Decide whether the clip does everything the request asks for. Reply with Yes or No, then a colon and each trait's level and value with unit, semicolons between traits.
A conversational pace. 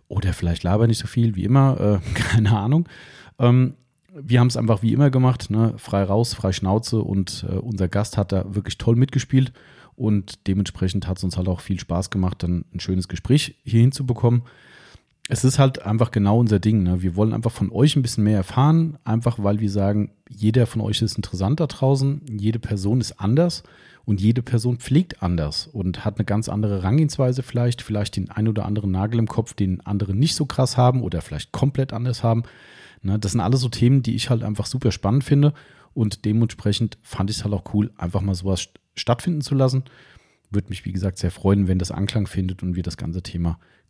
No: fast, 210 wpm